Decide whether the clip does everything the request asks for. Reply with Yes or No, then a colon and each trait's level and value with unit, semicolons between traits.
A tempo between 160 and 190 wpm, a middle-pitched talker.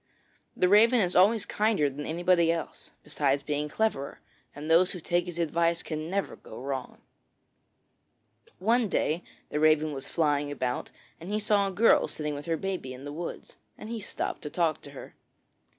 Yes: average, 180 wpm; medium, 165 Hz